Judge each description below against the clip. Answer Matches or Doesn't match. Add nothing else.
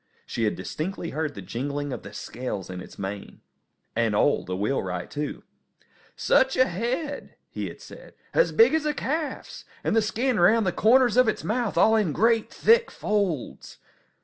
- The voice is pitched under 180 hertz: Doesn't match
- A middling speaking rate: Matches